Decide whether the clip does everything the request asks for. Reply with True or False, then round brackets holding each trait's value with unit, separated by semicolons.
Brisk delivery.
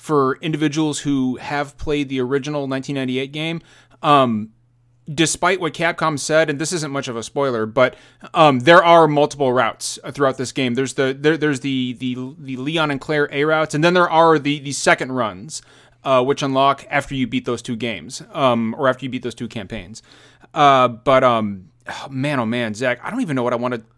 True (210 wpm)